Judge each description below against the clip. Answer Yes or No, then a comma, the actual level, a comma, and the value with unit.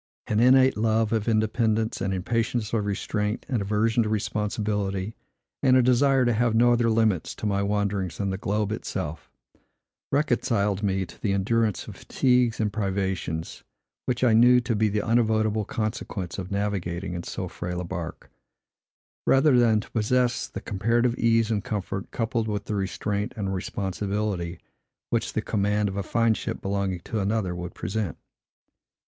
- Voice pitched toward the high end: No, low, 105 Hz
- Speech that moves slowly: No, average, 165 wpm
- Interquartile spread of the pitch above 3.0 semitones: No, average, 2.7 semitones